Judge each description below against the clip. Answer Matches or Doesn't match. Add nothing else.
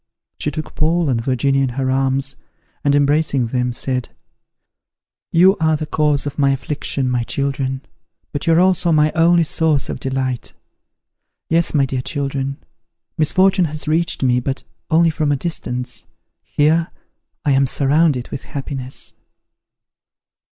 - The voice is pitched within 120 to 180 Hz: Matches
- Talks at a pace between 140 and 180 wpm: Matches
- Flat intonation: Doesn't match